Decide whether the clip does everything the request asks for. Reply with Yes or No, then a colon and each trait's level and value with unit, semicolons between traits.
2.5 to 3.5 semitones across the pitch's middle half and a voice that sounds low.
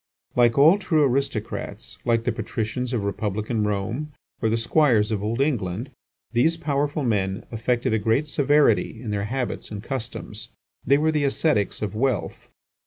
No: average, 4.9 semitones; low, 120 Hz